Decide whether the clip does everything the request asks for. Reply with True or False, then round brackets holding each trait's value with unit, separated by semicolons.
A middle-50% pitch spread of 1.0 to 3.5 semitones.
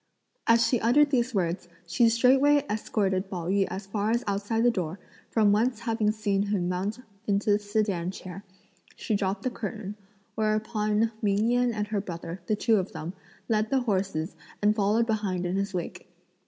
True (2.8 semitones)